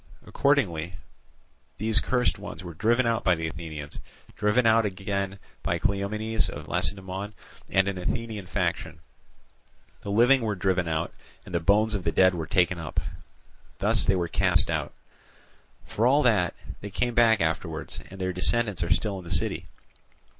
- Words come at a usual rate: Yes, average, 160 wpm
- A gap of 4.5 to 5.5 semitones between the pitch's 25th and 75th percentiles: No, average, 4.0 semitones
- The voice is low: Yes, low, 100 Hz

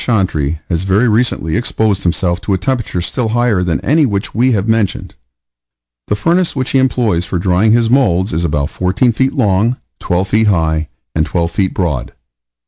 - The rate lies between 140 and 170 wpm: No, average, 180 wpm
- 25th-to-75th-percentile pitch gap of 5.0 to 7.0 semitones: Yes, average, 5.3 semitones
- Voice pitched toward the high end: No, low, 100 Hz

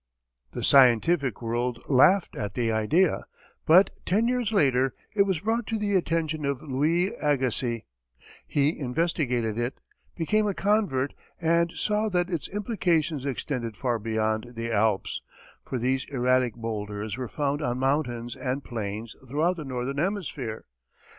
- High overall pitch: No, low, 135 Hz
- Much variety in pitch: Yes, wide, 6.2 semitones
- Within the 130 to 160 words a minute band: Yes, average, 140 wpm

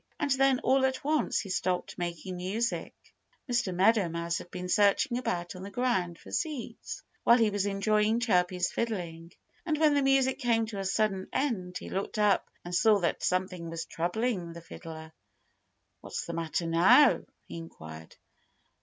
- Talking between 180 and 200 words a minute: No, average, 170 wpm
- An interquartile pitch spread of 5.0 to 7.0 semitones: Yes, average, 5.3 semitones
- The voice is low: No, high, 195 Hz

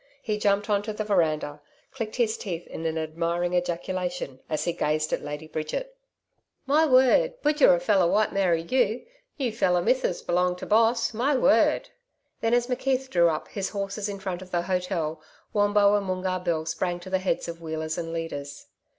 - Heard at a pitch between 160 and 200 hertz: Yes, medium, 185 Hz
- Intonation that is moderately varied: Yes, average, 4.4 semitones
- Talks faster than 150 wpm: Yes, average, 185 wpm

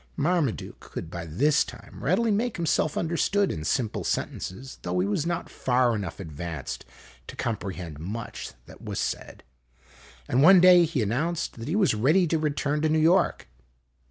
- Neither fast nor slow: Yes, average, 165 wpm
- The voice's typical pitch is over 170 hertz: No, medium, 140 Hz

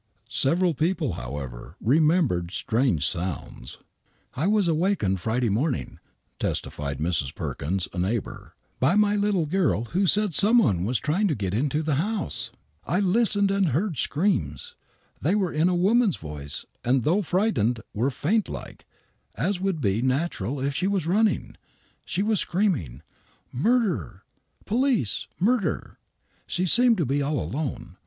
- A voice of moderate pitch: Yes, medium, 155 Hz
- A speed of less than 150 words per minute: No, average, 155 wpm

